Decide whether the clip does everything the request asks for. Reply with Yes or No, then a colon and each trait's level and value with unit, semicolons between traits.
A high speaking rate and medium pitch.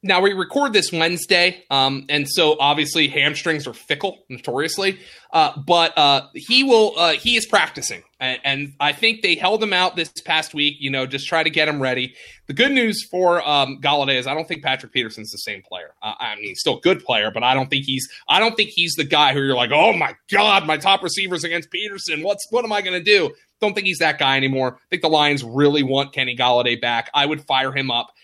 Yes: fast, 235 wpm; medium, 155 Hz